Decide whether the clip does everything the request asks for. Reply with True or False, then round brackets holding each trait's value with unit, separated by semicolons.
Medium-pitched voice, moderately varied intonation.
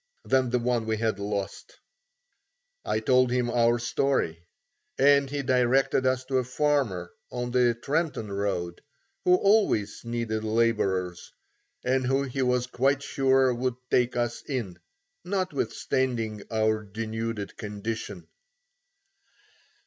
False (120 Hz; 3.2 semitones)